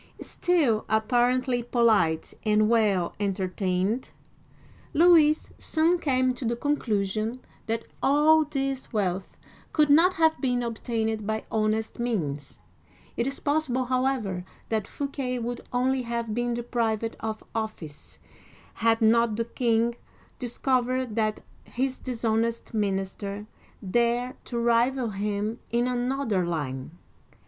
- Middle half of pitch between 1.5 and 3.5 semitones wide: Yes, average, 3.1 semitones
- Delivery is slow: Yes, slow, 120 wpm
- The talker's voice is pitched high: Yes, high, 235 Hz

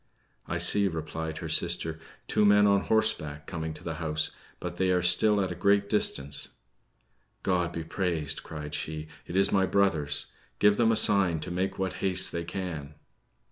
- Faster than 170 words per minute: Yes, average, 180 wpm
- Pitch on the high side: No, very low, 90 Hz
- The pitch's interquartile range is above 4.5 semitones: No, average, 3.8 semitones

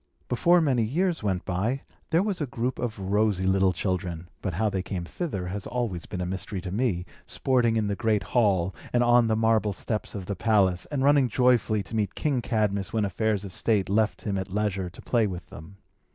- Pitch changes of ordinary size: Yes, average, 4.1 semitones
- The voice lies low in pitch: Yes, low, 105 Hz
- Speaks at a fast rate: Yes, fast, 210 wpm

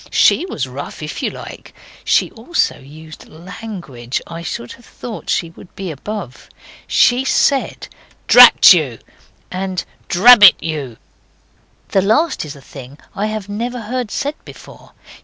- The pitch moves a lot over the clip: Yes, wide, 7.0 semitones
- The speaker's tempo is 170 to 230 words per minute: No, average, 140 wpm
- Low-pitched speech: No, medium, 185 Hz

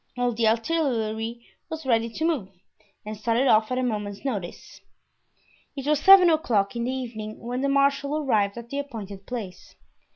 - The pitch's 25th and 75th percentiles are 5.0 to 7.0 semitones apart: No, average, 4.4 semitones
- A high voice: Yes, high, 235 Hz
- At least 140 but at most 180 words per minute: Yes, average, 170 wpm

